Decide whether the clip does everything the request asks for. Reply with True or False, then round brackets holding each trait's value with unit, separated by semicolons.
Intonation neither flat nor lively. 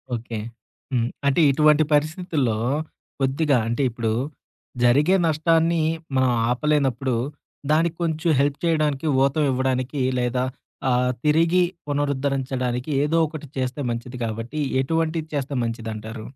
True (3.7 semitones)